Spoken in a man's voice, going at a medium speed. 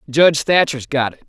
Yes: male; average, 190 wpm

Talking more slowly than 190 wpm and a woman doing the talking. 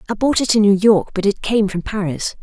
No: fast, 270 wpm; female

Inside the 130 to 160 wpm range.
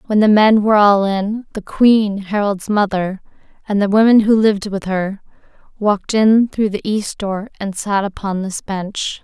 No: average, 180 wpm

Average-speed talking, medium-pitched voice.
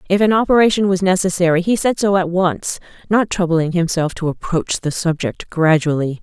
Yes: average, 175 wpm; medium, 180 Hz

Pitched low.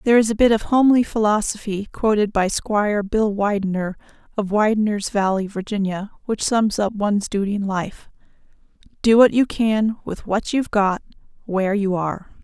No: high, 210 Hz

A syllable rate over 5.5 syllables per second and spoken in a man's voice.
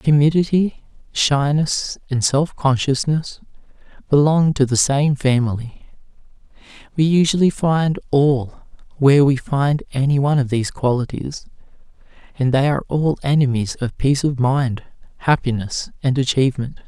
No: 4.7 syllables/s; male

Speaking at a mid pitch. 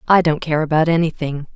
Yes: medium, 155 Hz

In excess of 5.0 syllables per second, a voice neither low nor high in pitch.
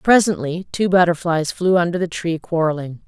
Yes: 5.2 syllables/s; medium, 170 Hz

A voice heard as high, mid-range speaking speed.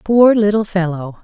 Yes: high, 195 Hz; average, 145 wpm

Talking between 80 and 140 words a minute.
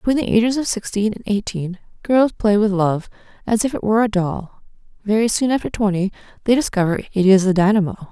No: average, 200 wpm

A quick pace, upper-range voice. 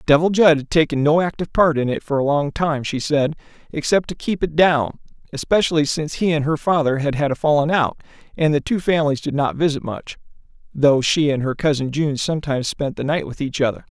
No: fast, 215 wpm; medium, 150 Hz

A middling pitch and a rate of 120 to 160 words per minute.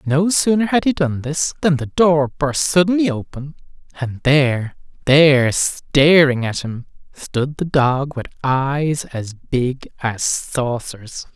Yes: medium, 145 Hz; average, 145 wpm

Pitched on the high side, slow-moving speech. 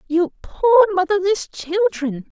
Yes: very high, 340 Hz; slow, 100 wpm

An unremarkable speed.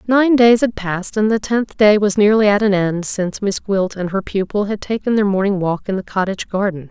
No: fast, 245 wpm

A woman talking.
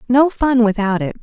Yes: female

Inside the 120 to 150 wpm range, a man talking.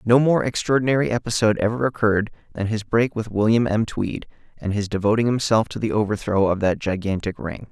No: average, 185 wpm; male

